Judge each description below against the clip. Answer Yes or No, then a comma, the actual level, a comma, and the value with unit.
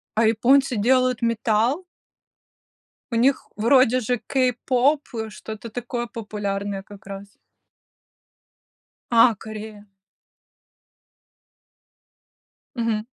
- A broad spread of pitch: No, average, 3.0 semitones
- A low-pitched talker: No, high, 230 Hz